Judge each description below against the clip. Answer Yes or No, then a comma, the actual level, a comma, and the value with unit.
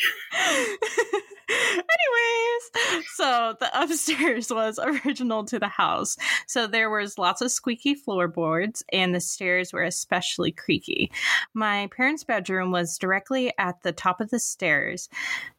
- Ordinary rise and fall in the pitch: No, wide, 8.9 semitones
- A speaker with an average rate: No, slow, 125 wpm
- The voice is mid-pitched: No, high, 235 Hz